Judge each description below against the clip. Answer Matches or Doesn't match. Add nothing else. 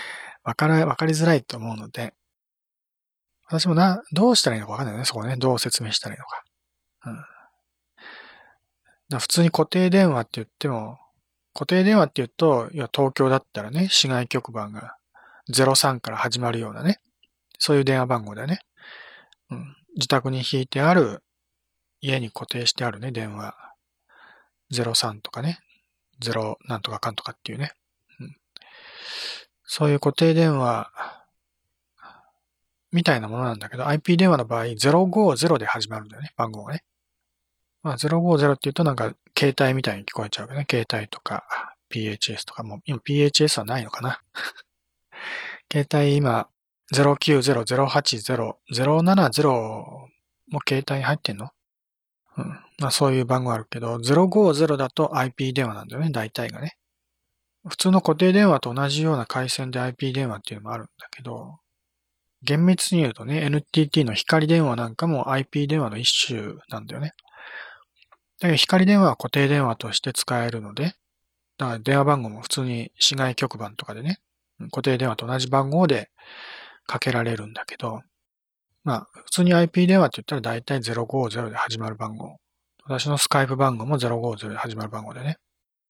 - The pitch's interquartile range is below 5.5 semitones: Matches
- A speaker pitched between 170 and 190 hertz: Doesn't match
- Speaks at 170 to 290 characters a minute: Doesn't match